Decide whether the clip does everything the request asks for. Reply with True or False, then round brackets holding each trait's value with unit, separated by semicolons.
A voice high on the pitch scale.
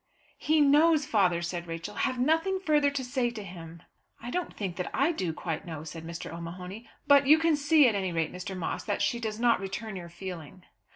True (205 Hz)